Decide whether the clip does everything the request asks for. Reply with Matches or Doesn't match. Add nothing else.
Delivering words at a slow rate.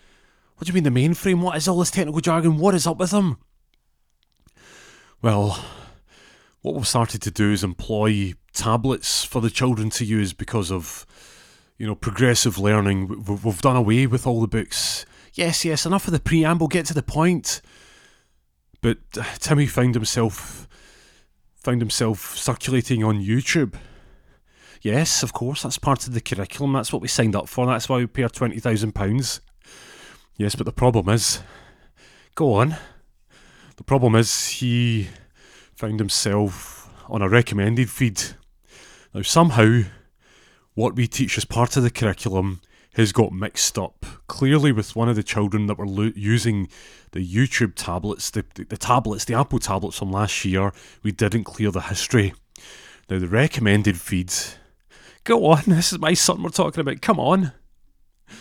Doesn't match